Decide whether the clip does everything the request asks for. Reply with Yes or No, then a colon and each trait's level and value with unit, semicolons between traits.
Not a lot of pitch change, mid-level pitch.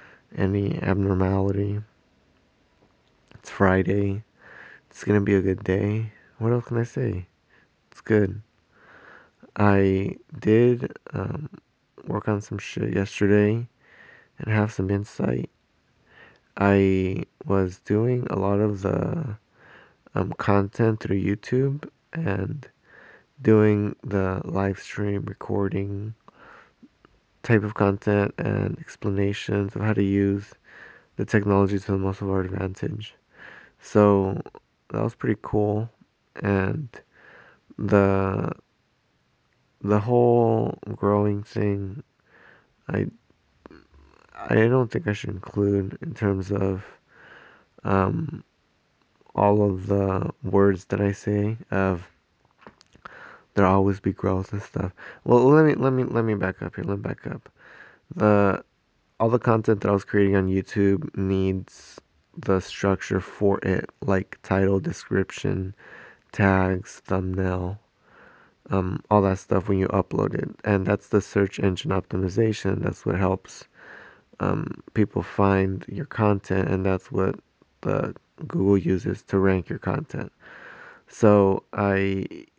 No: narrow, 1.7 semitones; low, 100 Hz